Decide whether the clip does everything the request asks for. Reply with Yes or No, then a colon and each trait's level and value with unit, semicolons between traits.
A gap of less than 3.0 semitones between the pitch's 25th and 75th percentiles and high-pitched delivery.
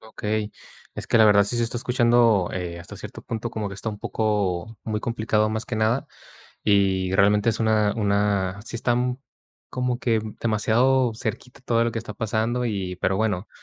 No: narrow, 2.4 semitones; low, 110 Hz